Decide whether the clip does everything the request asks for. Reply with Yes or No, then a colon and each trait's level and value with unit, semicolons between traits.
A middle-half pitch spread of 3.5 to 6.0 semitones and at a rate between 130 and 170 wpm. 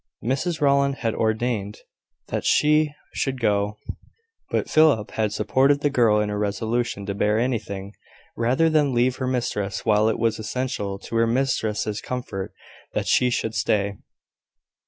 Yes: average, 3.8 semitones; average, 150 wpm